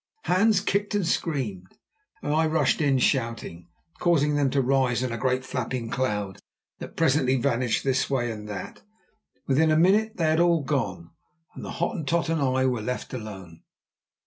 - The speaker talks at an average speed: Yes, average, 170 wpm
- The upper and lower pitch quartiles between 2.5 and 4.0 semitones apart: No, wide, 5.4 semitones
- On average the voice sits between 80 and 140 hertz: Yes, low, 135 Hz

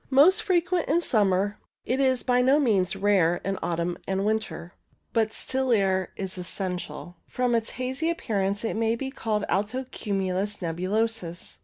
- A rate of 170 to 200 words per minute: No, average, 155 wpm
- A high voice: Yes, high, 210 Hz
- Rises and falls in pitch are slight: No, average, 5.1 semitones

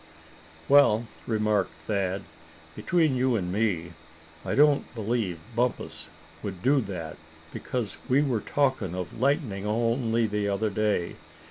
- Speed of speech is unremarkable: No, slow, 125 wpm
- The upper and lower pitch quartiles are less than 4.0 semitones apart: No, average, 4.4 semitones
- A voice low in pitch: Yes, low, 110 Hz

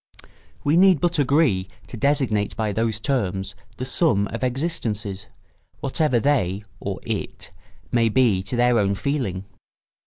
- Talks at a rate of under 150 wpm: Yes, slow, 135 wpm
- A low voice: Yes, low, 120 Hz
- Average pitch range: No, wide, 5.7 semitones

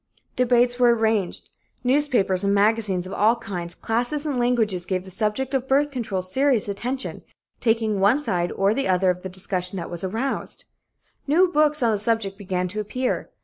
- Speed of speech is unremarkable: Yes, average, 180 wpm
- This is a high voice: Yes, high, 220 Hz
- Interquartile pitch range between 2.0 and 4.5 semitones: No, average, 4.9 semitones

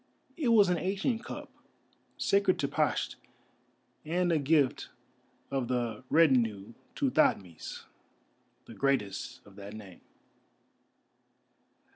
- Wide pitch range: Yes, wide, 8.9 semitones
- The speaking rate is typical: No, slow, 105 wpm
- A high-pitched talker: No, low, 135 Hz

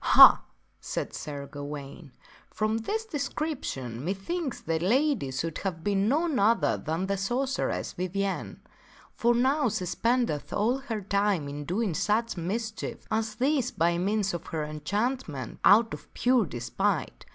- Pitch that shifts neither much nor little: No, wide, 6.8 semitones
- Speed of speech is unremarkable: Yes, average, 150 wpm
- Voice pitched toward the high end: Yes, high, 200 Hz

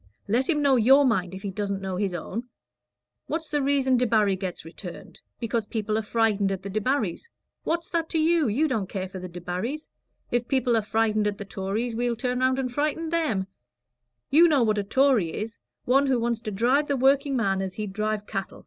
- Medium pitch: No, high, 225 Hz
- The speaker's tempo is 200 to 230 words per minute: Yes, fast, 205 wpm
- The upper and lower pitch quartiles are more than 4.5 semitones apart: Yes, average, 5.2 semitones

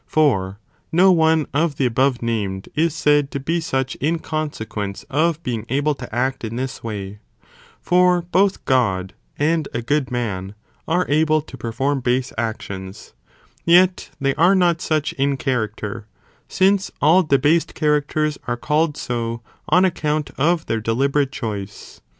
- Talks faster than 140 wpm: Yes, average, 150 wpm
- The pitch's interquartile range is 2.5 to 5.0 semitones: No, wide, 5.5 semitones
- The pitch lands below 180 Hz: Yes, medium, 140 Hz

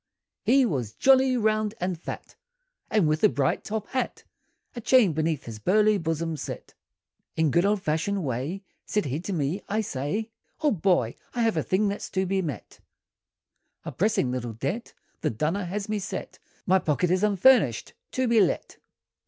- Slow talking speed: No, average, 175 wpm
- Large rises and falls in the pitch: Yes, wide, 5.8 semitones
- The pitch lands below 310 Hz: Yes, high, 190 Hz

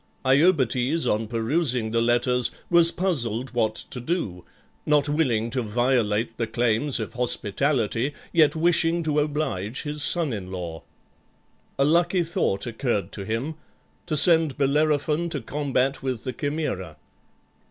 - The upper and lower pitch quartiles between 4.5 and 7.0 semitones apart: Yes, average, 5.2 semitones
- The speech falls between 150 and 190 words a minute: No, slow, 135 wpm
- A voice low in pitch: Yes, low, 130 Hz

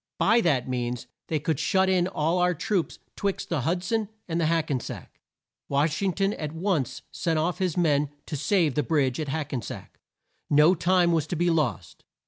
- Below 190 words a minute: No, fast, 205 wpm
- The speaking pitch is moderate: Yes, medium, 165 Hz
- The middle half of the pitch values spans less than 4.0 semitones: Yes, average, 3.5 semitones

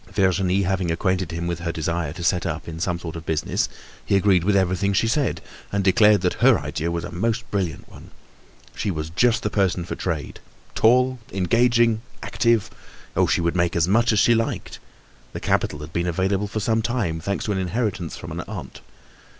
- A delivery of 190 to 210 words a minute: Yes, average, 200 wpm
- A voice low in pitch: Yes, very low, 95 Hz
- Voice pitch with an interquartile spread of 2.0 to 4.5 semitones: Yes, average, 4.0 semitones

